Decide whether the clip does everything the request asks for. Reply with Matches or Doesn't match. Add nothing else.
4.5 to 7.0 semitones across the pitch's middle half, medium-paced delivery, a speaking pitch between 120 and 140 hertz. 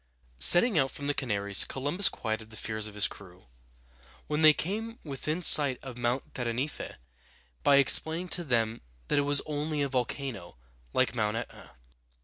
Matches